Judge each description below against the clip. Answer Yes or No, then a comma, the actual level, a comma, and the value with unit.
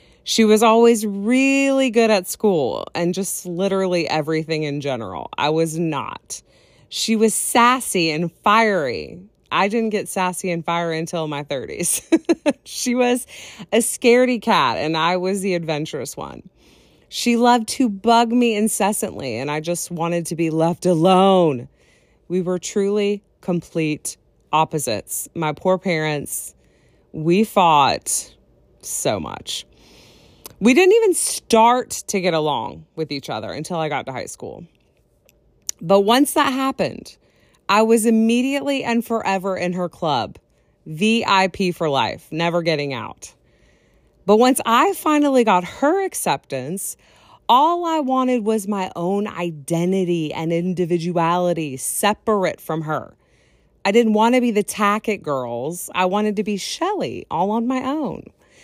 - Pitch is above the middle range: Yes, high, 195 Hz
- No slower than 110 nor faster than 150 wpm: Yes, average, 140 wpm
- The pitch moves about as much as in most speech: No, wide, 5.7 semitones